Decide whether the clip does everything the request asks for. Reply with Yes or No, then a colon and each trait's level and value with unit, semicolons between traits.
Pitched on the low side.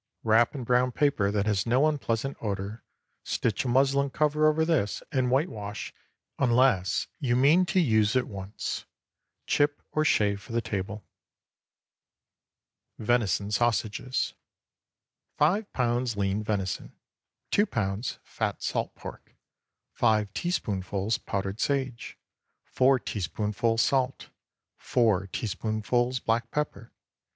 Yes: low, 115 Hz